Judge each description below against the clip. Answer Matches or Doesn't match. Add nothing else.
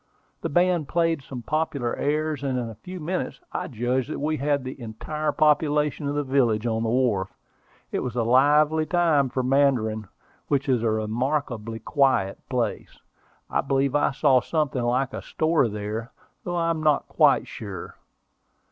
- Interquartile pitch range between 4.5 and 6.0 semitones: Doesn't match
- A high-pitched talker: Doesn't match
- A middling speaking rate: Matches